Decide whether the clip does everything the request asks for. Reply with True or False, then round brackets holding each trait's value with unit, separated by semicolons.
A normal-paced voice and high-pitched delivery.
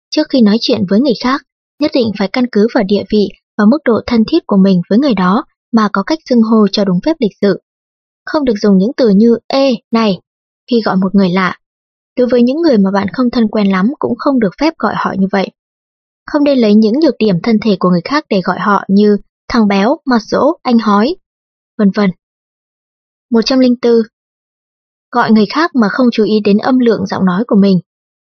True (220 wpm; 220 Hz)